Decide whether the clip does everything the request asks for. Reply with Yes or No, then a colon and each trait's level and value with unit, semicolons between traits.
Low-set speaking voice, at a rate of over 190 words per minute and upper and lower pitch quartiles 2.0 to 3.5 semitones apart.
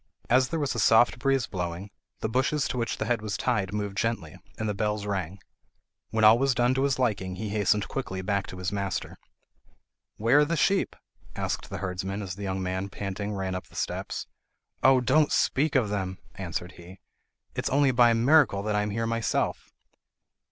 No: low, 105 Hz; average, 200 wpm; average, 4.4 semitones